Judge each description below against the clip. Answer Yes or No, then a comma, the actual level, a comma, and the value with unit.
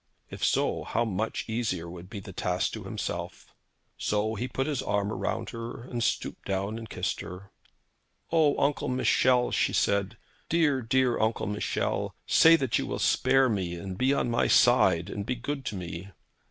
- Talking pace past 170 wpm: Yes, average, 180 wpm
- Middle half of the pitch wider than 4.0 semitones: Yes, average, 4.6 semitones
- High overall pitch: No, low, 115 Hz